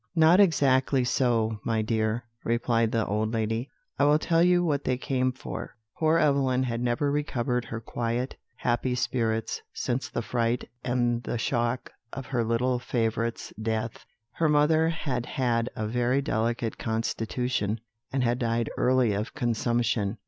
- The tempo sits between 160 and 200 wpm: No, average, 150 wpm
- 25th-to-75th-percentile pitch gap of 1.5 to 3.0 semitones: Yes, narrow, 2.4 semitones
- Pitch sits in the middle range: No, low, 120 Hz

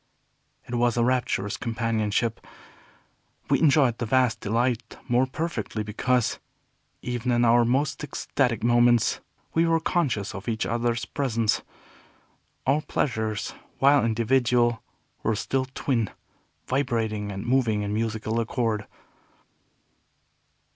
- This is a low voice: Yes, low, 120 Hz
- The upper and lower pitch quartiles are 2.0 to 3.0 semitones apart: Yes, narrow, 2.6 semitones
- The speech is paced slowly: Yes, slow, 115 wpm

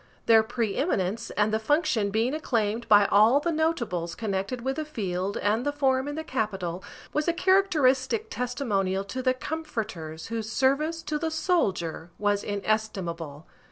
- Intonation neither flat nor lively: No, wide, 6.4 semitones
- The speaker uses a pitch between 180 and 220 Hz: No, high, 230 Hz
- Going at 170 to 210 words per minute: No, average, 155 wpm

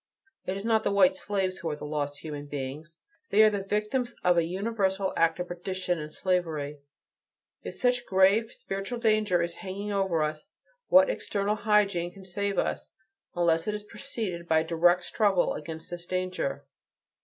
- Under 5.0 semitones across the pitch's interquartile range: Yes, average, 3.7 semitones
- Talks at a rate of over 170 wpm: Yes, average, 180 wpm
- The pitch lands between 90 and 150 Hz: No, medium, 185 Hz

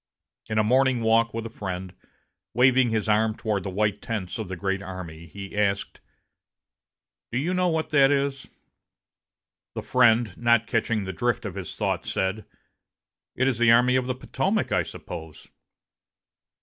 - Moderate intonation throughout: Yes, average, 4.2 semitones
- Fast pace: No, average, 160 wpm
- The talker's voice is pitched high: No, low, 110 Hz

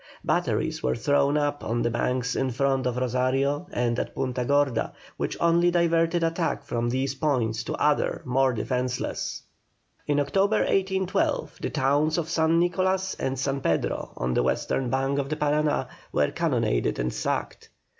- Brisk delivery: No, average, 160 wpm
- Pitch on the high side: No, medium, 140 Hz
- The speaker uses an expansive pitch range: No, average, 4.3 semitones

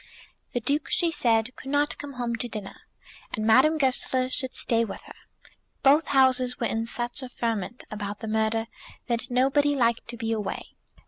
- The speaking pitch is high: Yes, high, 245 Hz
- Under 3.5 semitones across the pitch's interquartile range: Yes, average, 3.0 semitones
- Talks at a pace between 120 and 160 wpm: No, average, 180 wpm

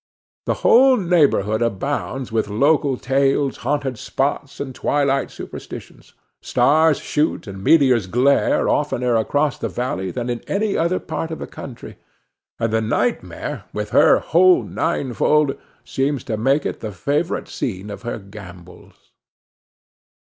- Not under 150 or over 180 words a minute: No, slow, 135 wpm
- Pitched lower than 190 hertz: Yes, low, 135 Hz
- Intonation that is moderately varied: Yes, average, 4.7 semitones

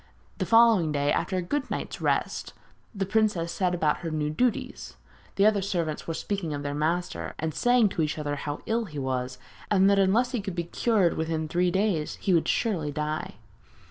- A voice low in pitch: No, medium, 175 Hz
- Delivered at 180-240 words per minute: Yes, average, 200 wpm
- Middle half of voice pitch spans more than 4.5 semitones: Yes, average, 5.0 semitones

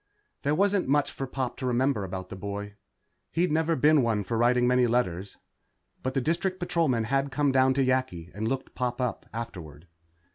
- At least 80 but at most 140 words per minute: No, average, 185 wpm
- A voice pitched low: Yes, low, 125 Hz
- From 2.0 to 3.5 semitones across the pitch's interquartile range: No, average, 4.3 semitones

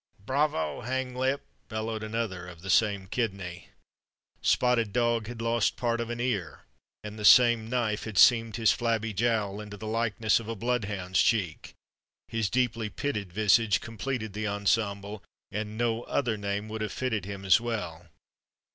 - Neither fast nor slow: Yes, average, 155 wpm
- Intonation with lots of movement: No, narrow, 2.6 semitones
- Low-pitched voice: Yes, low, 110 Hz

